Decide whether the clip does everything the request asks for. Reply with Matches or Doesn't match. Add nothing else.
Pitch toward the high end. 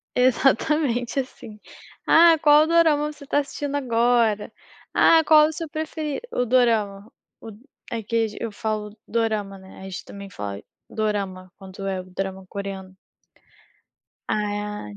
Matches